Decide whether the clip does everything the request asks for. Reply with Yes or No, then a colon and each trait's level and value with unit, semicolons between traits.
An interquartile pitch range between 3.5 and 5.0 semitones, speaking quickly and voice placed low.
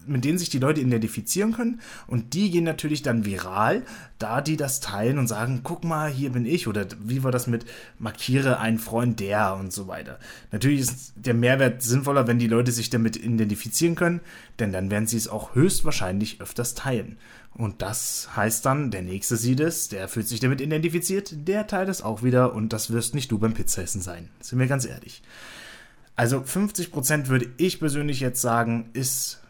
Yes: average, 4.5 semitones; fast, 195 wpm; low, 125 Hz